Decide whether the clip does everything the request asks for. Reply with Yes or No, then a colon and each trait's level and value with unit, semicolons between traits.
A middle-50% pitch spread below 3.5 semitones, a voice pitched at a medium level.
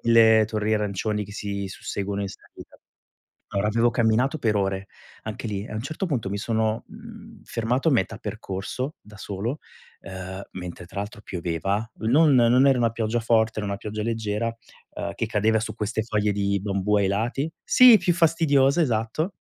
No: average, 2.9 semitones; low, 110 Hz